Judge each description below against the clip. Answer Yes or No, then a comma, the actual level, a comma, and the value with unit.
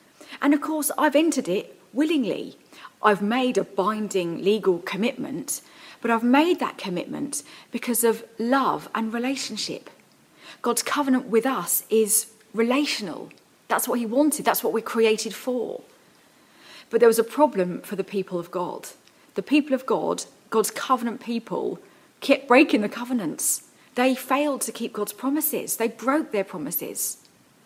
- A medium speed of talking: Yes, average, 150 wpm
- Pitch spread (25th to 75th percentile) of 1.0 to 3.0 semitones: No, average, 4.0 semitones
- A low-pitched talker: No, high, 240 Hz